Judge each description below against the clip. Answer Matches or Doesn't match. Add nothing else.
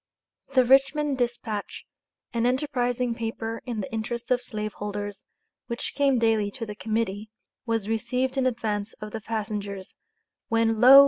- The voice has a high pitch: Matches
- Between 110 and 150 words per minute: Matches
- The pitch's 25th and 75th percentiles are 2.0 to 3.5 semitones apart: Matches